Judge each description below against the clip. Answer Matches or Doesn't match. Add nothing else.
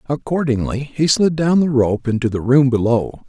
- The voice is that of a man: Matches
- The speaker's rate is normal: Matches